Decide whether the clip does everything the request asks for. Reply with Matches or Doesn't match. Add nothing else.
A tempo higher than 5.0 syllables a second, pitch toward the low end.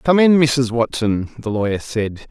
Doesn't match